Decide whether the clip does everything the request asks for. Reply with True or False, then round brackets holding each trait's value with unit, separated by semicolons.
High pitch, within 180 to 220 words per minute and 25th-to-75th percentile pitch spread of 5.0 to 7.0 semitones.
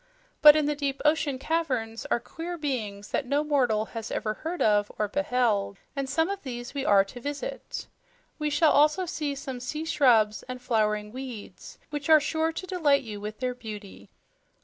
True (265 Hz; 185 wpm; 5.4 semitones)